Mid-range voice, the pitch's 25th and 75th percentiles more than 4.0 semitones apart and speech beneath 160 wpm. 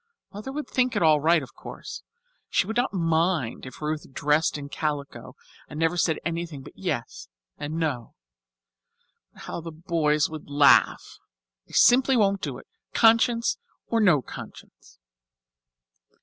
Yes: medium, 160 Hz; average, 5.0 semitones; average, 150 wpm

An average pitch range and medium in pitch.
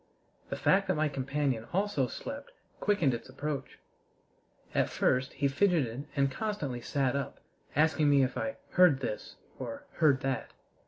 No: wide, 5.8 semitones; medium, 145 Hz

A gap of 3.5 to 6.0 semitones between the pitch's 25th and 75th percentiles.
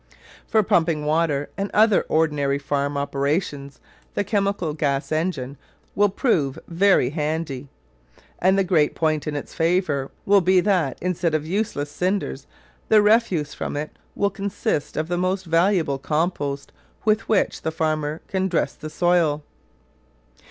Yes: average, 4.4 semitones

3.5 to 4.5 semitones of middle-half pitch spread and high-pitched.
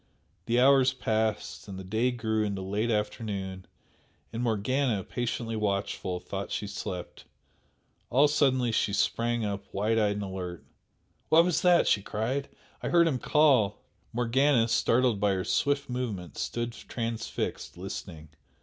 No: average, 4.1 semitones; low, 115 Hz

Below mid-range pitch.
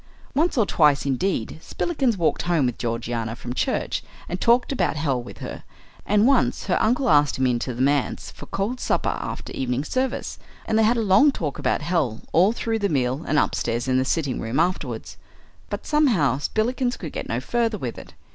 No: medium, 165 Hz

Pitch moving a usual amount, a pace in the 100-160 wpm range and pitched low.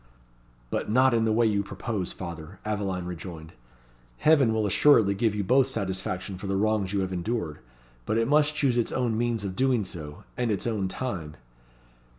No: average, 4.1 semitones; average, 180 wpm; low, 105 Hz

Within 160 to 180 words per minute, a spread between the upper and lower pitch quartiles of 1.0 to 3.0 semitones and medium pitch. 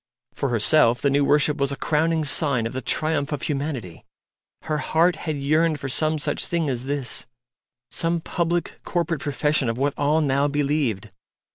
Yes: average, 170 wpm; narrow, 2.5 semitones; medium, 145 Hz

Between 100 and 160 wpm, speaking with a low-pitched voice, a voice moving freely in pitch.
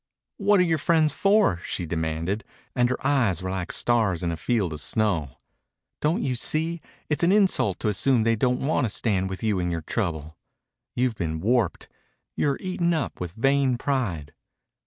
No: average, 180 wpm; low, 115 Hz; wide, 7.8 semitones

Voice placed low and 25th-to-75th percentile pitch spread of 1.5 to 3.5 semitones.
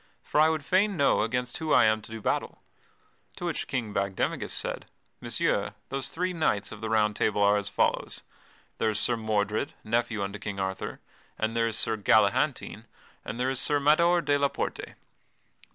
No: low, 115 Hz; average, 5.1 semitones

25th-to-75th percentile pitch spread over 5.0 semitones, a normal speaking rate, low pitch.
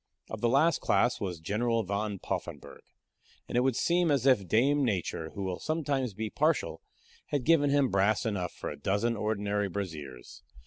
Yes: wide, 5.5 semitones; average, 175 wpm; low, 110 Hz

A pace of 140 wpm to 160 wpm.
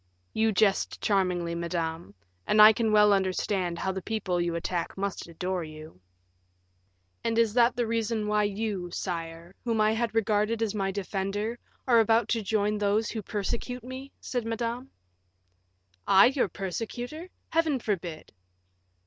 Yes: average, 150 wpm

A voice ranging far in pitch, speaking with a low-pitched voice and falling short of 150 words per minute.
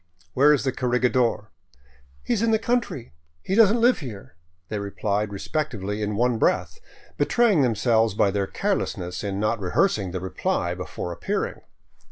No: wide, 6.8 semitones; low, 110 Hz; average, 170 wpm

